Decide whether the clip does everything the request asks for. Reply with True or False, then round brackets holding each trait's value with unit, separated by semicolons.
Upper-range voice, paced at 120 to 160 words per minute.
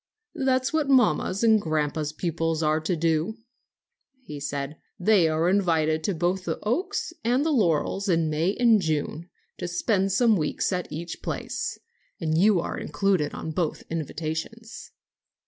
False (175 Hz; 155 wpm)